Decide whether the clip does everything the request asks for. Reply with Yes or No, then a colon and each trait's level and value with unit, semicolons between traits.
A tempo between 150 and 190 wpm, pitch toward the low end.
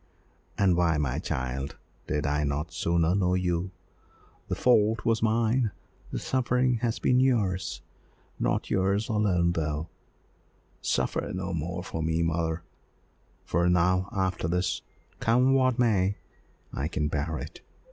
No: slow, 135 wpm; very low, 90 Hz